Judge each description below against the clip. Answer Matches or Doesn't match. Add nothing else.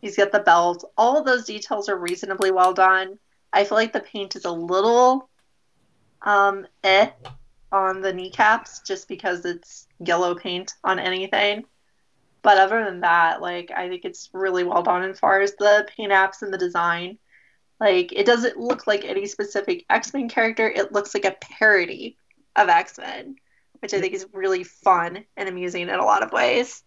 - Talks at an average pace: Matches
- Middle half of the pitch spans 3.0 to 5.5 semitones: Matches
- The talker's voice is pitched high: Matches